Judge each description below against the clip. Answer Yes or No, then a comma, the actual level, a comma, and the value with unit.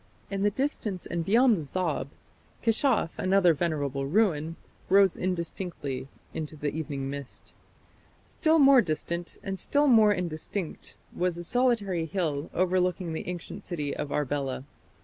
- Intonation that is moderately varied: Yes, average, 4.7 semitones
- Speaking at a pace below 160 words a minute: Yes, slow, 135 wpm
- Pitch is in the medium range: Yes, medium, 175 Hz